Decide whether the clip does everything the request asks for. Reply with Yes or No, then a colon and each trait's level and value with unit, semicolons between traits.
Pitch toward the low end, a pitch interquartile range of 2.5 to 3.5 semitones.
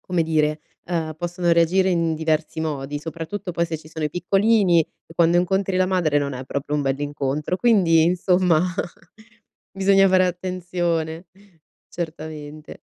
No: medium, 165 Hz; average, 2.8 semitones